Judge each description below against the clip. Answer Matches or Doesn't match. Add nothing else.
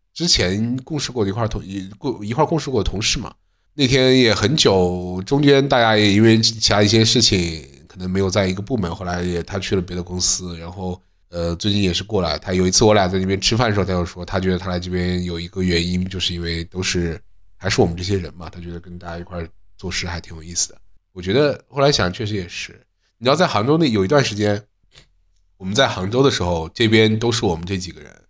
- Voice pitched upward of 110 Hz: Doesn't match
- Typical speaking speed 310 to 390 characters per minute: Matches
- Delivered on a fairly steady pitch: Doesn't match